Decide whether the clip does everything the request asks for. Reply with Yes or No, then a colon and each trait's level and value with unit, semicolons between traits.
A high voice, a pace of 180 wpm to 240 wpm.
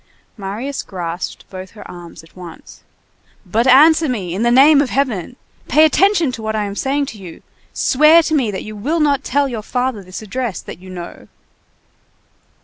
Yes: high, 235 Hz; average, 185 wpm